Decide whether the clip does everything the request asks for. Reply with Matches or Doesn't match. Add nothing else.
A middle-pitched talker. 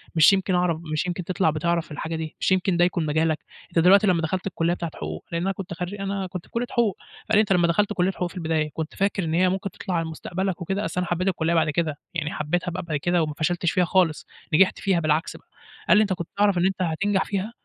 Matches